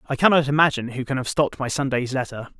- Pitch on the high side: No, low, 135 Hz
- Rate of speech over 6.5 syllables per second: Yes, 7.0 syllables/s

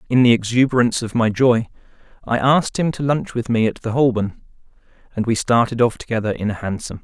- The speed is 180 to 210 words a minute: Yes, fast, 205 wpm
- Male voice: Yes, male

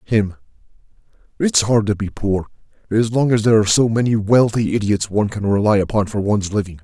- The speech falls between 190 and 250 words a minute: Yes, average, 195 wpm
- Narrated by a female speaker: No, male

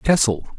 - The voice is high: No, low, 130 Hz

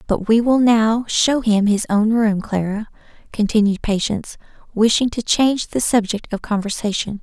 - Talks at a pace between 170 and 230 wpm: No, average, 160 wpm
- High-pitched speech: Yes, high, 220 Hz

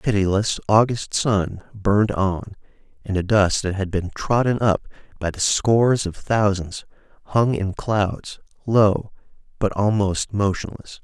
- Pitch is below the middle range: Yes, low, 105 Hz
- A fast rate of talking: No, average, 140 wpm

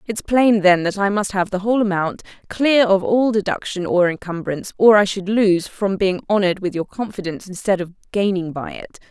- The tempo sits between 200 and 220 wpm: Yes, fast, 205 wpm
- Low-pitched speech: No, high, 195 Hz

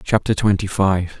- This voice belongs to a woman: No, male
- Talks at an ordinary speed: Yes, average, 150 wpm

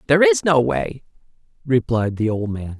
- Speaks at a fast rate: No, average, 170 wpm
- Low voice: Yes, low, 125 Hz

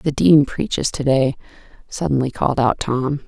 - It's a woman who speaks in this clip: Yes, female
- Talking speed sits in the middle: Yes, average, 165 wpm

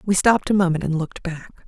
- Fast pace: Yes, fast, 250 wpm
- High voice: No, medium, 180 Hz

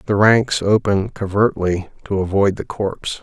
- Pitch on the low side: Yes, low, 100 Hz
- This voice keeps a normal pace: Yes, average, 150 wpm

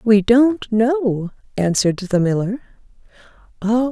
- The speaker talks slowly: Yes, slow, 90 wpm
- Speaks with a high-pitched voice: Yes, high, 220 Hz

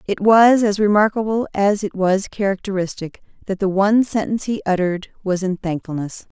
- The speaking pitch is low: No, high, 200 Hz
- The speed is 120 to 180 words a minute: Yes, average, 160 wpm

